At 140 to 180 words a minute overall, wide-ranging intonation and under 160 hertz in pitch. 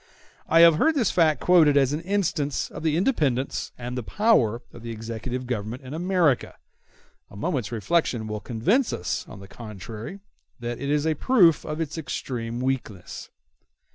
Yes: average, 170 wpm; wide, 6.1 semitones; low, 135 Hz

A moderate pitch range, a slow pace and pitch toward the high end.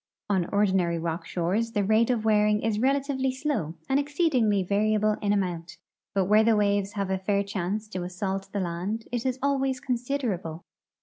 No: average, 3.8 semitones; average, 175 wpm; high, 210 Hz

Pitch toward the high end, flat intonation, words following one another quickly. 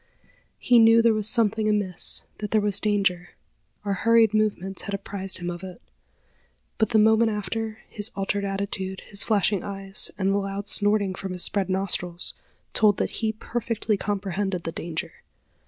No: high, 200 Hz; narrow, 2.0 semitones; average, 165 wpm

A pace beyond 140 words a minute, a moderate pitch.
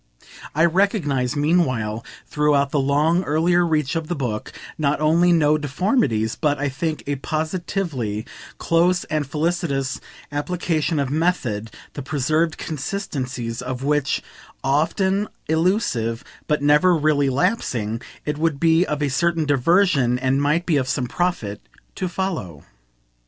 No: slow, 135 wpm; medium, 150 Hz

